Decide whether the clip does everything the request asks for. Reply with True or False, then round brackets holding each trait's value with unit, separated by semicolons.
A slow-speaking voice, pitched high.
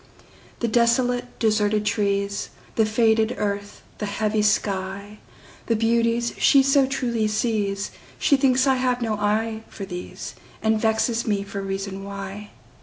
True (120 wpm; 215 Hz)